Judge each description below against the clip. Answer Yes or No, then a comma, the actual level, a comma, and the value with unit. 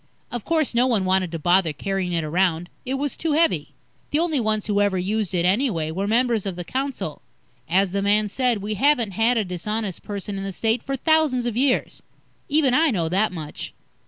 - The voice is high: Yes, high, 210 Hz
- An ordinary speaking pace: No, fast, 210 wpm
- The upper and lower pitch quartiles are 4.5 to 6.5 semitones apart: Yes, wide, 5.4 semitones